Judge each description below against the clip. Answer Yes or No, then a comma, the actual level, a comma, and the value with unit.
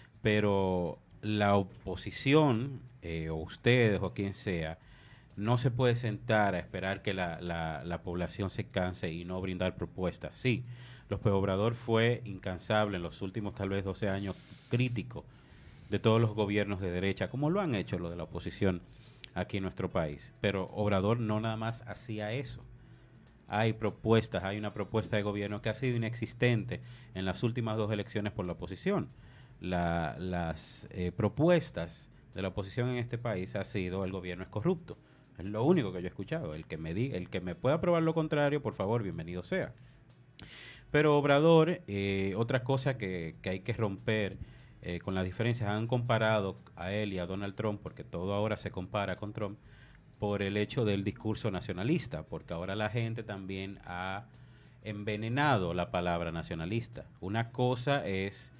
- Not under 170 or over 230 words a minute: Yes, average, 175 wpm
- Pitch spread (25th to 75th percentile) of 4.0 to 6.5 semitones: Yes, average, 4.3 semitones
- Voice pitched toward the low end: Yes, low, 105 Hz